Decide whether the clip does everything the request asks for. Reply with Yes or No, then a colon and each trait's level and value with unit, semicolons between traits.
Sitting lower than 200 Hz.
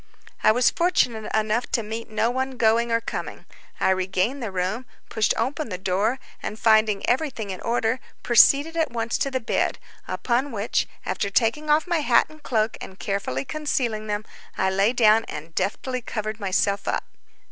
No: high, 225 Hz